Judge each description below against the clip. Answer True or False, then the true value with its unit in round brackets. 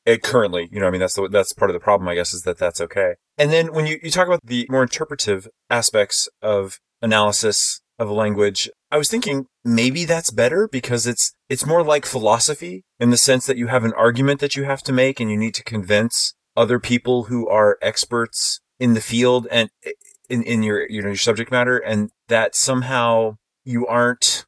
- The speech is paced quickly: True (215 wpm)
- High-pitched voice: False (120 Hz)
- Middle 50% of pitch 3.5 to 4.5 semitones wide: True (4.2 semitones)